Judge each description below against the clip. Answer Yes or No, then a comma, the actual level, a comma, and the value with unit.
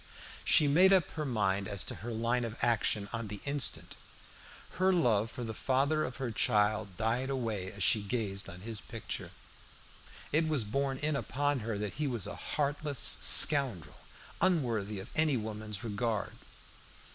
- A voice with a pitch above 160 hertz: No, low, 115 Hz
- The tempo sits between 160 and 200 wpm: Yes, average, 165 wpm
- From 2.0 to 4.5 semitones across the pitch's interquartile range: No, average, 5.1 semitones